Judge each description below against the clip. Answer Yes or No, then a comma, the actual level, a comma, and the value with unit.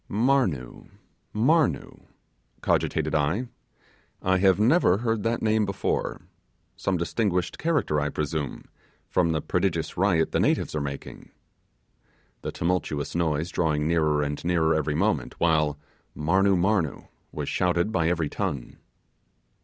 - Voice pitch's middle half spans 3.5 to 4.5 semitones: No, average, 4.9 semitones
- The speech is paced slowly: Yes, slow, 125 wpm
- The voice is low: Yes, very low, 85 Hz